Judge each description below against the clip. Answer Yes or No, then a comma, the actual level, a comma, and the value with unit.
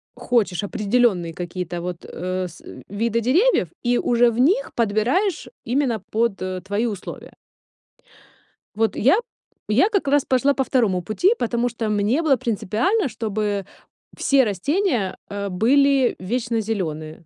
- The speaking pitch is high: Yes, high, 225 Hz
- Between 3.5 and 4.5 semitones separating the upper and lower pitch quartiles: No, average, 4.9 semitones